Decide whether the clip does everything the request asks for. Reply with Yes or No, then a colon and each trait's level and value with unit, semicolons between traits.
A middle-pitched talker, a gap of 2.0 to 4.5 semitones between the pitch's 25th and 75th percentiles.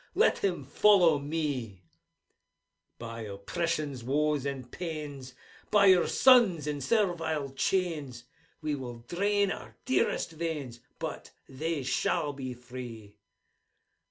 No: medium, 145 Hz; average, 5.0 semitones